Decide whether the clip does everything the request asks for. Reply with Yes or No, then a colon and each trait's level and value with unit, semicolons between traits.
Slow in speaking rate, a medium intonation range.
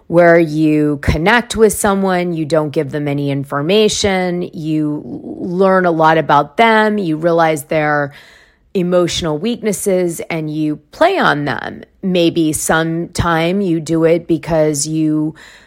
Yes: slow, 130 wpm; average, 3.3 semitones